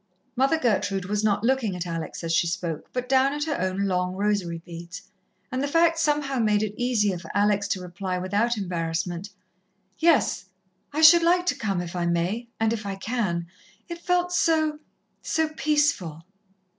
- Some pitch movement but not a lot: No, wide, 7.8 semitones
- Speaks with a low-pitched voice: No, high, 210 Hz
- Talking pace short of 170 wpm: No, average, 175 wpm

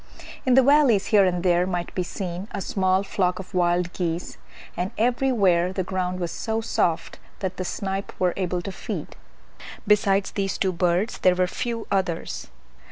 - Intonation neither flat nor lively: No, narrow, 2.1 semitones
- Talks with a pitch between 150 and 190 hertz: Yes, medium, 185 Hz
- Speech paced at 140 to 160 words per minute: No, average, 170 wpm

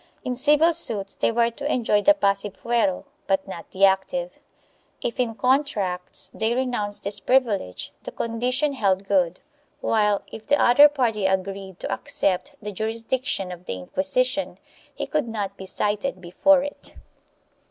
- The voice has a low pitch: No, high, 220 Hz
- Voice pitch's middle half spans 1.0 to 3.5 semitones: No, average, 5.1 semitones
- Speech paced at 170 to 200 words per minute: No, average, 155 wpm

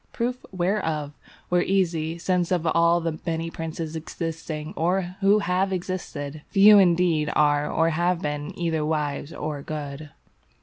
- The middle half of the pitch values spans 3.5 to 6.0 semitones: No, average, 2.8 semitones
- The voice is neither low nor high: Yes, medium, 165 Hz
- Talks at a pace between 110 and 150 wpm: Yes, average, 140 wpm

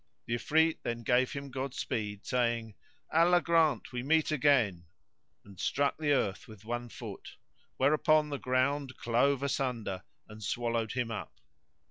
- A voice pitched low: Yes, low, 125 Hz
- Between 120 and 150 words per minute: Yes, average, 140 wpm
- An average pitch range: Yes, average, 3.8 semitones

